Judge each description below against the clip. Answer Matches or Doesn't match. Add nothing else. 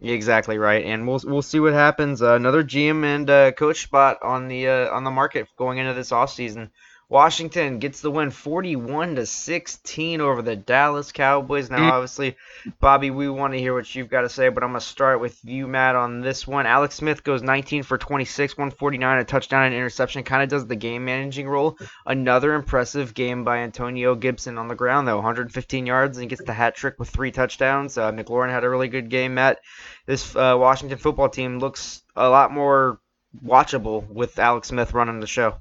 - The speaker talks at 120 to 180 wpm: Doesn't match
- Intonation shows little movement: Matches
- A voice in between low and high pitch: Doesn't match